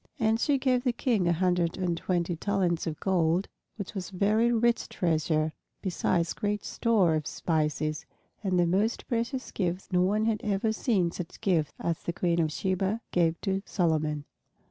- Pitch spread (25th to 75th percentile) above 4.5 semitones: No, average, 4.2 semitones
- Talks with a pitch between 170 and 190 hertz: Yes, medium, 185 Hz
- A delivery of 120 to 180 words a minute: Yes, average, 175 wpm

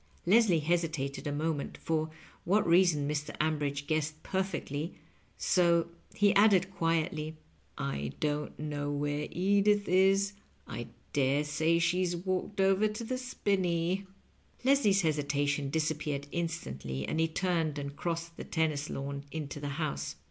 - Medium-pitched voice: Yes, medium, 160 Hz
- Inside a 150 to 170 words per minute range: No, average, 140 wpm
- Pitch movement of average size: Yes, average, 4.2 semitones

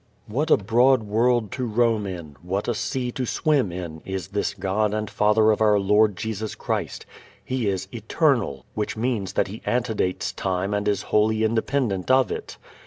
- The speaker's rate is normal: Yes, average, 175 wpm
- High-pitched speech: No, low, 105 Hz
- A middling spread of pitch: Yes, average, 3.4 semitones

